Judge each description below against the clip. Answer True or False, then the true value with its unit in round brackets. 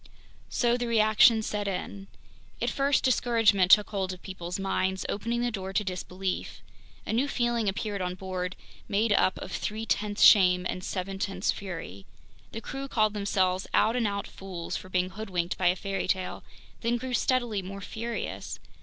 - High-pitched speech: True (200 Hz)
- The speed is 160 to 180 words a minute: True (170 wpm)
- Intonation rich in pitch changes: False (3.3 semitones)